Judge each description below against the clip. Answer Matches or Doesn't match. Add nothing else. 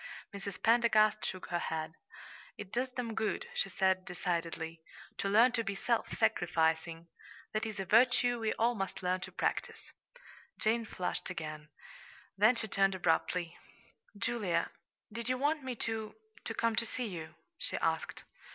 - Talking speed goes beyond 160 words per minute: Doesn't match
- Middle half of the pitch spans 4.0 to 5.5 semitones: Matches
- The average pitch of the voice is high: Matches